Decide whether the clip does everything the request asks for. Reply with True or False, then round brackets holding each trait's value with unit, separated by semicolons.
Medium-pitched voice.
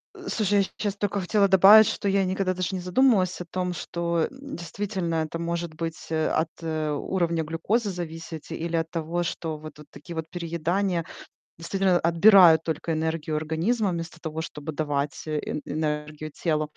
True (170 Hz)